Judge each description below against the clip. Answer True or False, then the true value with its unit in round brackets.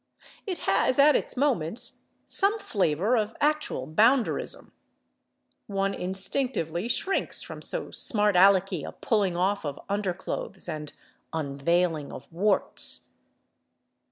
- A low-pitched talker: False (195 Hz)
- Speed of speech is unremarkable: False (110 wpm)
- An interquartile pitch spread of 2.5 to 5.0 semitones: False (5.6 semitones)